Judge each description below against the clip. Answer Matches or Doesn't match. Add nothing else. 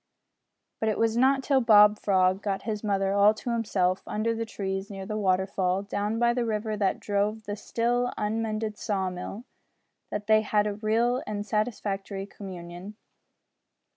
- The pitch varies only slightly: Matches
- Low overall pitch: Doesn't match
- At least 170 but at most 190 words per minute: Doesn't match